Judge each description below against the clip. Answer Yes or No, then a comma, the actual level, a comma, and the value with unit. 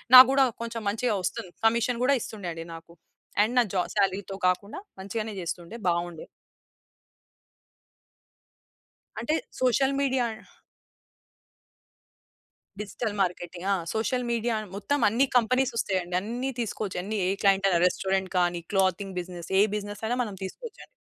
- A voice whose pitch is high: Yes, high, 205 Hz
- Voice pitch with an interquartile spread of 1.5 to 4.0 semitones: No, average, 4.6 semitones